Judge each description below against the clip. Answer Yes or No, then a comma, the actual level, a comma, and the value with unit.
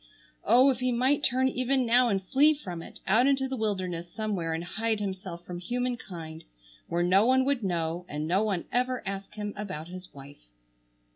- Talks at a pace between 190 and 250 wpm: Yes, average, 195 wpm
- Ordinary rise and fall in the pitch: No, wide, 6.1 semitones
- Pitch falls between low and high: No, high, 205 Hz